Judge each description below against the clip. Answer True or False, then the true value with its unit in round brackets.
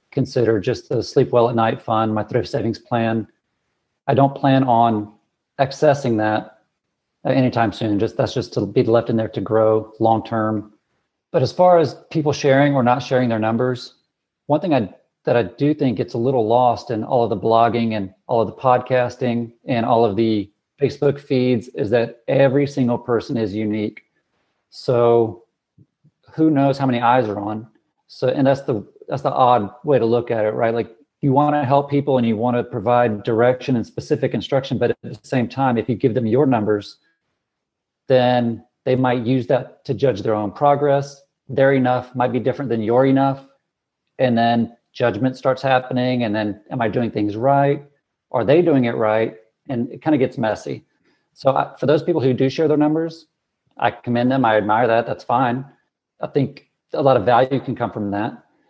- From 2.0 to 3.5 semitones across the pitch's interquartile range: True (3.1 semitones)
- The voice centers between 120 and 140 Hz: True (125 Hz)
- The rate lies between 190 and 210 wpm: True (195 wpm)